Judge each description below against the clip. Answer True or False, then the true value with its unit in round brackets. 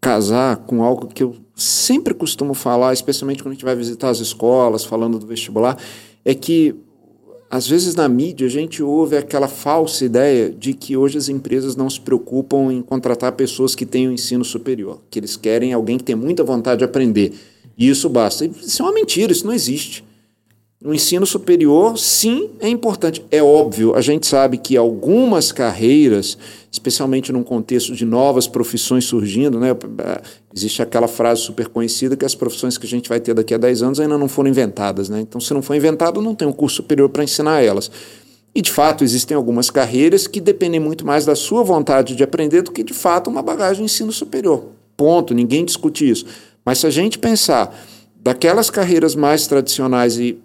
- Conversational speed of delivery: False (195 wpm)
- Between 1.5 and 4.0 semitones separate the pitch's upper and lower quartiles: False (4.5 semitones)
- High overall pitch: False (130 Hz)